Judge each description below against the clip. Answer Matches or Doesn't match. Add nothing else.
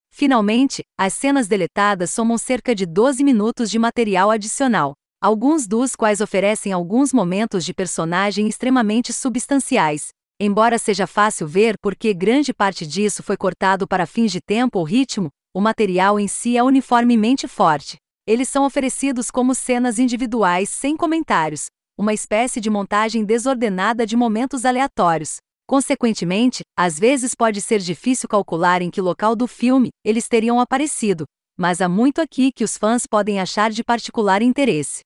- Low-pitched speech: Doesn't match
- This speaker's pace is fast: Doesn't match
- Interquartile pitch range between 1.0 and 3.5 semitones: Doesn't match